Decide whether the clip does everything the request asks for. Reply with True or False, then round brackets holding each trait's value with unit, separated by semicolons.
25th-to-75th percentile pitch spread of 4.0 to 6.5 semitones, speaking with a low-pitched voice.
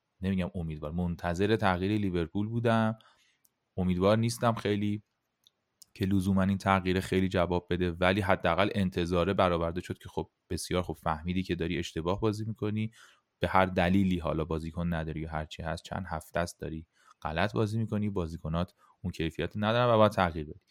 False (3.1 semitones; 95 Hz)